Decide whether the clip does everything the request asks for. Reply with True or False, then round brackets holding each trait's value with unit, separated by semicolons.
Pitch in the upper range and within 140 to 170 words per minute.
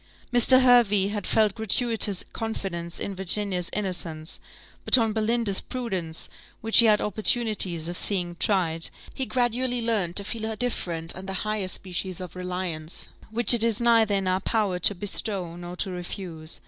True (200 Hz; 160 wpm)